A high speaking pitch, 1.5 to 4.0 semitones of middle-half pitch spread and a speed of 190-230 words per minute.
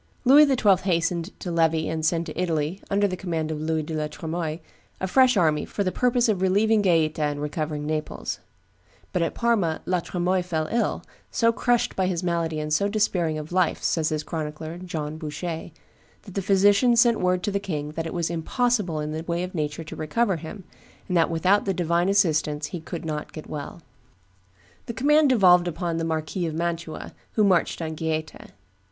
No: medium, 170 Hz; average, 3.7 semitones; average, 195 wpm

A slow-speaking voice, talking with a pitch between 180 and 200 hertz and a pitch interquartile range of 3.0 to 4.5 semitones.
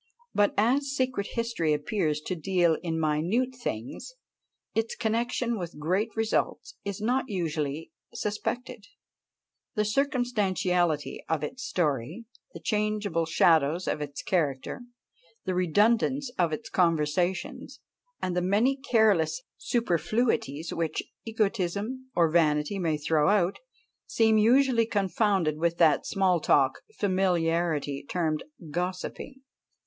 No: slow, 115 wpm; medium, 185 Hz; wide, 5.6 semitones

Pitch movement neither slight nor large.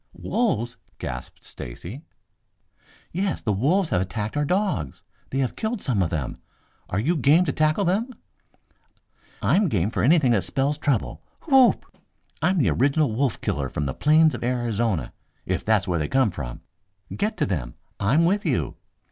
No: wide, 9.0 semitones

